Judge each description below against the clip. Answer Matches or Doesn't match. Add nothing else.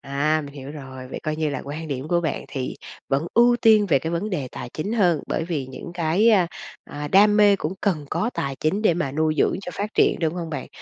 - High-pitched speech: Doesn't match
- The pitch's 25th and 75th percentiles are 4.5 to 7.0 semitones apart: Matches